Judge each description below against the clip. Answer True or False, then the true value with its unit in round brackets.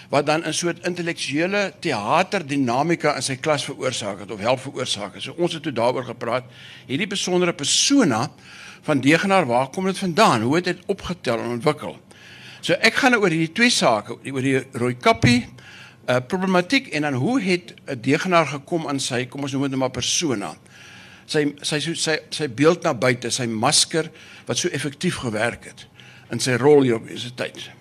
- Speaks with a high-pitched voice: False (150 Hz)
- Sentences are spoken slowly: False (185 wpm)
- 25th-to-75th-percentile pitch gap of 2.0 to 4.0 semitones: False (5.4 semitones)